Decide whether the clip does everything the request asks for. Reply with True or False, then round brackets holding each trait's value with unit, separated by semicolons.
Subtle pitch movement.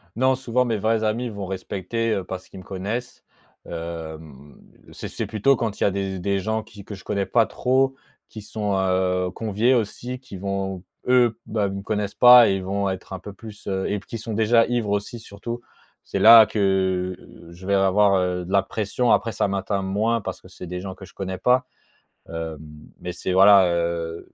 False (3.2 semitones)